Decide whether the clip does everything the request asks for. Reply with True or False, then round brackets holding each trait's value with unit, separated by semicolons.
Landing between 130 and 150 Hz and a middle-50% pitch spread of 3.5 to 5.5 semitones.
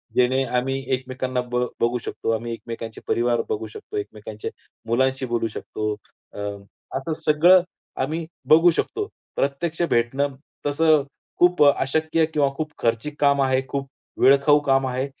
True (135 Hz; 4.0 semitones)